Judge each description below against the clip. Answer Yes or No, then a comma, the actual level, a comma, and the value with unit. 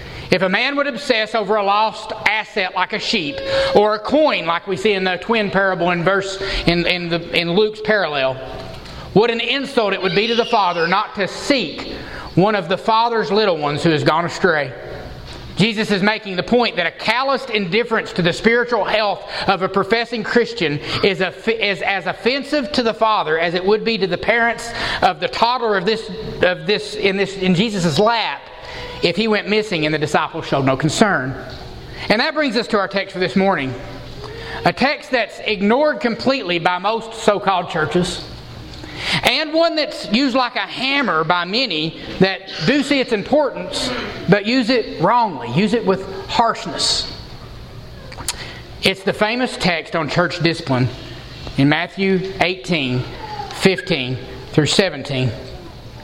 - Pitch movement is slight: No, average, 4.5 semitones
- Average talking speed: Yes, average, 170 wpm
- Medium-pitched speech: No, high, 195 Hz